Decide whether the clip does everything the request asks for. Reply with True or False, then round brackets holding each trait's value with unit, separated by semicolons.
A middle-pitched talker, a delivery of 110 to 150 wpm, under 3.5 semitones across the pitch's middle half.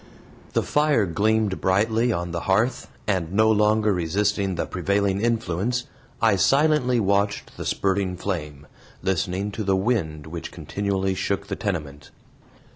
False (100 Hz; 135 wpm; 3.1 semitones)